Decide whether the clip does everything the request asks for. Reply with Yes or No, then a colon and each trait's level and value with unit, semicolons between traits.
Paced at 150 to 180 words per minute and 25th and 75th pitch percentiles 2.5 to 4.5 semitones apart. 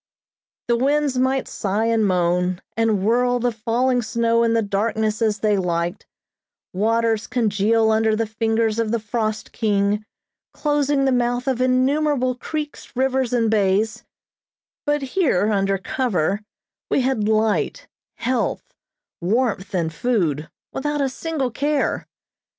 No: slow, 135 wpm; average, 3.5 semitones